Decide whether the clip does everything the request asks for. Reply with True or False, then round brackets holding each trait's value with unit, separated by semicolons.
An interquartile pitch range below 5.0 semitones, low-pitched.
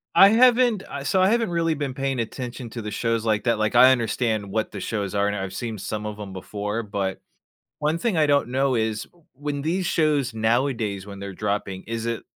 False (5.5 semitones; 115 Hz)